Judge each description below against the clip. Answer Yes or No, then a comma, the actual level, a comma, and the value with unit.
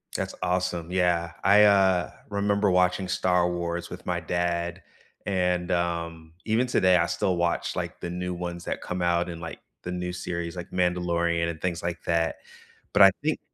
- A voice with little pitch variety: Yes, narrow, 1.2 semitones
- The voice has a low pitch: Yes, very low, 90 Hz